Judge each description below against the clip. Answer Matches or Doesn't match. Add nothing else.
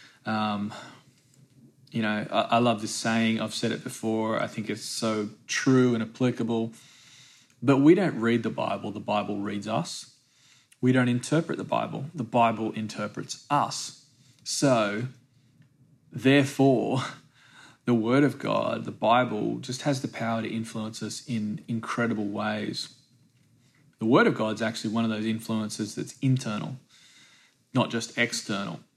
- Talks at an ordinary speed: Matches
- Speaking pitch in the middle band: Doesn't match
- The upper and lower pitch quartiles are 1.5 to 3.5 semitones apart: Matches